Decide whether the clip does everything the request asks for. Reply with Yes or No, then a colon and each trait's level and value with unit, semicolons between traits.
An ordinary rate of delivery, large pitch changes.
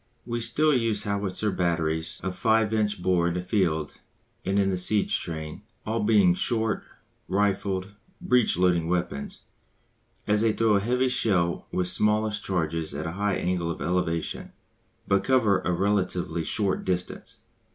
No: average, 150 wpm; average, 3.5 semitones